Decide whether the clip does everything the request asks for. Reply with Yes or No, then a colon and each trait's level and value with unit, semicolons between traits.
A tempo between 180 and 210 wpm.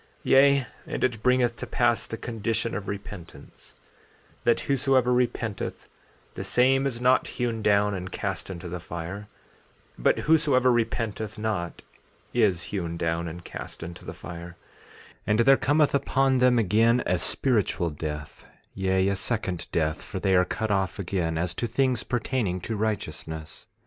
No: average, 155 wpm